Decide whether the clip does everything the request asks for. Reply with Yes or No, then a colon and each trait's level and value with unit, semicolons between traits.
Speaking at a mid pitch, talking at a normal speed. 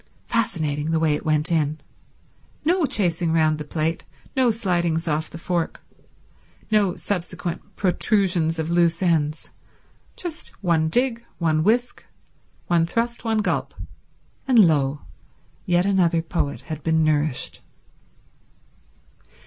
No: medium, 170 Hz; slow, 115 wpm